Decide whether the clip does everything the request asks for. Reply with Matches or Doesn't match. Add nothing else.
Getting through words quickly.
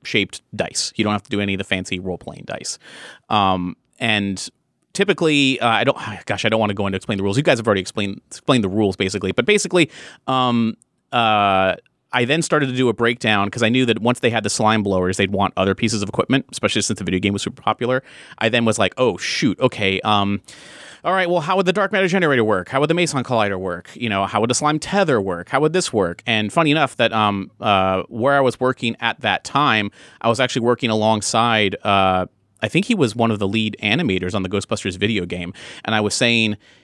Matches